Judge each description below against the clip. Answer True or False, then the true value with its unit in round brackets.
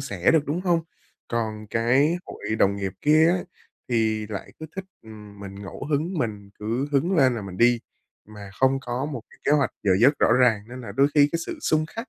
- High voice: False (120 Hz)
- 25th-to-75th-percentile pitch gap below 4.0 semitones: False (5.4 semitones)